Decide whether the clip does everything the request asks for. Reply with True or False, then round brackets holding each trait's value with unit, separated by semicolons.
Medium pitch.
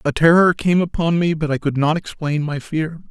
True (160 Hz)